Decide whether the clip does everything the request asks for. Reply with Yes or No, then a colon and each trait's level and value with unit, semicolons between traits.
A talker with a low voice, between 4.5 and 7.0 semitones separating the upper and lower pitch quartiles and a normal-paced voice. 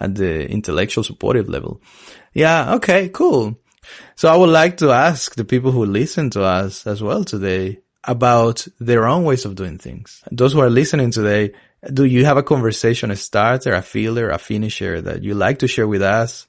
Yes: low, 115 Hz; average, 5.0 semitones; average, 195 wpm